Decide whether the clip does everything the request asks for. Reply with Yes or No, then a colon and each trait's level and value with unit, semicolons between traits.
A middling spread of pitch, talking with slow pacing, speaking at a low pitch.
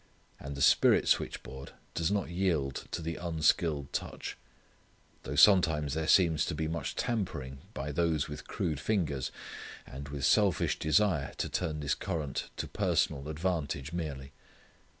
No: average, 3.4 semitones; average, 145 wpm; very low, 75 Hz